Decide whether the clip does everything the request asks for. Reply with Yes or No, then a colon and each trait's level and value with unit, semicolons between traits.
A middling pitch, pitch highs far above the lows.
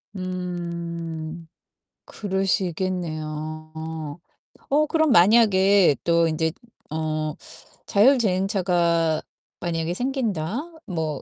No: medium, 170 Hz; average, 3.3 semitones